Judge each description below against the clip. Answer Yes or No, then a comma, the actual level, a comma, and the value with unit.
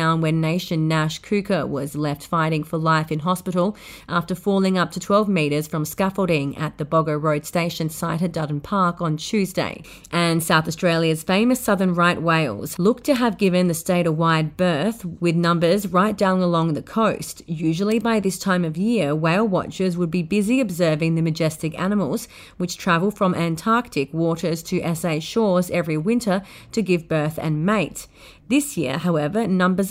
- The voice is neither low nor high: Yes, medium, 175 Hz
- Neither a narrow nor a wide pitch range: Yes, average, 3.2 semitones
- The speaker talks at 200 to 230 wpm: No, average, 175 wpm